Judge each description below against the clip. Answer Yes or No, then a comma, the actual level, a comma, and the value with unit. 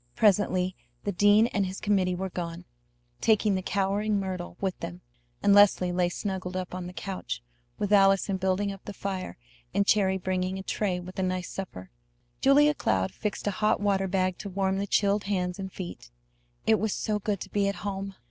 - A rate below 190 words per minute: No, average, 195 wpm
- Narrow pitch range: Yes, narrow, 1.8 semitones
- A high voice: Yes, high, 195 Hz